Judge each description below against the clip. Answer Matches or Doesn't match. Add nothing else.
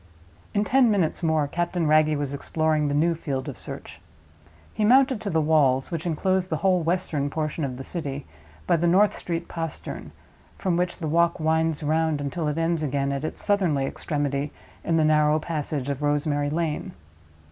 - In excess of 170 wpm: Matches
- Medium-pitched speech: Matches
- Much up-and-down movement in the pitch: Doesn't match